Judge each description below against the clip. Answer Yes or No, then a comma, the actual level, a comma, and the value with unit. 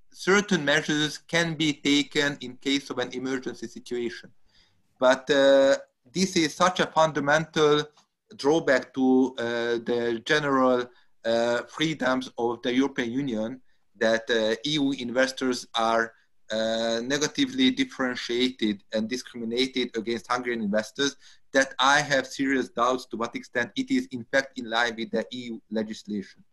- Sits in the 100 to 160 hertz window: Yes, low, 130 Hz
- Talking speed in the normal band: Yes, average, 135 wpm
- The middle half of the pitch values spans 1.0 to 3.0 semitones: No, average, 3.7 semitones